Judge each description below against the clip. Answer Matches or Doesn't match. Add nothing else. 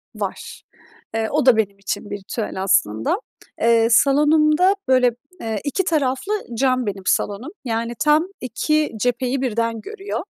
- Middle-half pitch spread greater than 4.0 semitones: Matches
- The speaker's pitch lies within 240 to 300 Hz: Matches